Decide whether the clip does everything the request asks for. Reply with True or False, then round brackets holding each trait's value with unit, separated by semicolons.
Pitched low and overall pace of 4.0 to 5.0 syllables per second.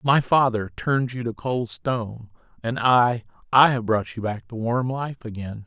True (120 Hz; 4.5 syllables/s)